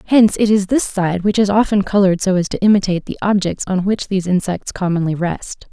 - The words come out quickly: Yes, fast, 220 wpm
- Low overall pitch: No, high, 195 Hz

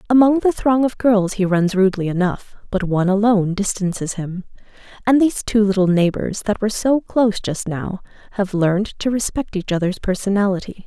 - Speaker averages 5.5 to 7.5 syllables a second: Yes, 5.6 syllables/s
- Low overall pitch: No, high, 200 Hz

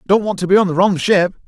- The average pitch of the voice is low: No, high, 190 Hz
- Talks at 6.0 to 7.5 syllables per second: Yes, 7.0 syllables/s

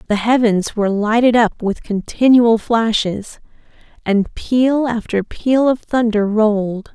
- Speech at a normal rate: No, slow, 130 wpm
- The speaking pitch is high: Yes, high, 225 Hz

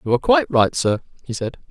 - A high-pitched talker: No, medium, 140 Hz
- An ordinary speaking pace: No, fast, 245 wpm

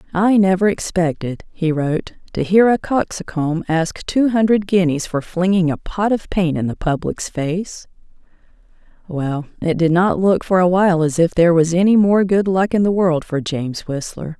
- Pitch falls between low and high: Yes, medium, 180 Hz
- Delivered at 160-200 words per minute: Yes, average, 190 wpm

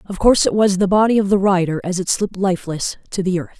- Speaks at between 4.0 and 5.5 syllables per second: No, 6.6 syllables/s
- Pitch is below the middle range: No, high, 190 Hz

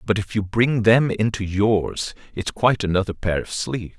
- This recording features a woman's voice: No, male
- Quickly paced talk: No, average, 195 wpm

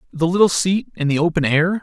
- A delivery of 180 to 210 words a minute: No, fast, 230 wpm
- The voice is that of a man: Yes, male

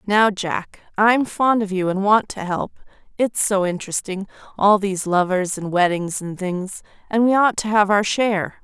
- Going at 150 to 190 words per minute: Yes, average, 180 wpm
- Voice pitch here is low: No, high, 200 Hz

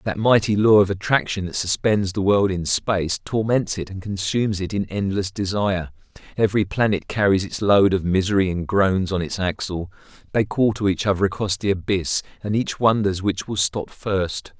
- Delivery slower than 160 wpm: No, average, 190 wpm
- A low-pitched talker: Yes, low, 100 Hz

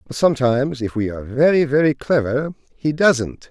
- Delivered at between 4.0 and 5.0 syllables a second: No, 5.4 syllables/s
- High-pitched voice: No, medium, 140 Hz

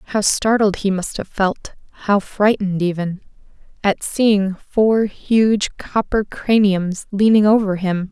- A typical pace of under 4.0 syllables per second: Yes, 3.7 syllables/s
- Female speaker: Yes, female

